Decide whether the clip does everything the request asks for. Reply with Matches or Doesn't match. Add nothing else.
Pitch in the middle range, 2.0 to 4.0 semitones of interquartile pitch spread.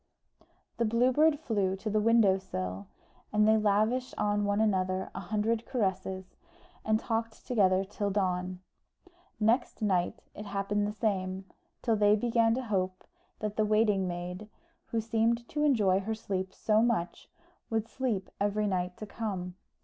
Doesn't match